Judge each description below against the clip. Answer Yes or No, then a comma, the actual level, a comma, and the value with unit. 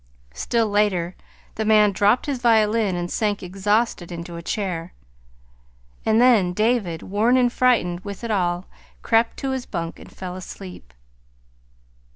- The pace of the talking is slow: No, average, 145 wpm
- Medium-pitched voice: No, high, 205 Hz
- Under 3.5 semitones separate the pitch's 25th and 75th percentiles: No, average, 4.3 semitones